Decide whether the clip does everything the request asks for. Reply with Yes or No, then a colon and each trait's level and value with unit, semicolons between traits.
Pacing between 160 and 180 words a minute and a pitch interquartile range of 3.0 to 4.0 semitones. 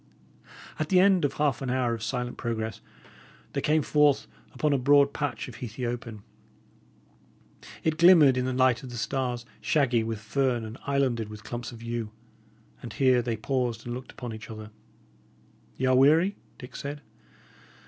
Yes: average, 170 wpm; average, 3.3 semitones